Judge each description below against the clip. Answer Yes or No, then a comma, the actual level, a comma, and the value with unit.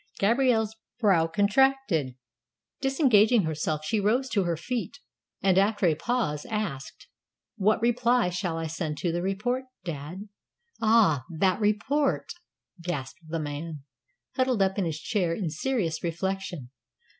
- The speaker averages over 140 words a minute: No, slow, 135 wpm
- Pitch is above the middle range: Yes, high, 195 Hz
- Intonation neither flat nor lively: No, wide, 5.9 semitones